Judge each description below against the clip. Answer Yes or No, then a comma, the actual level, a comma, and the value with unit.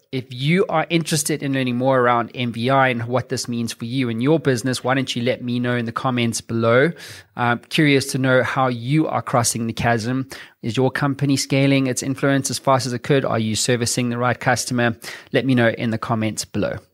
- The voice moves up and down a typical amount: No, narrow, 2.2 semitones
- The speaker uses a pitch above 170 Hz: No, low, 125 Hz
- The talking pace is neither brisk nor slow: No, fast, 220 wpm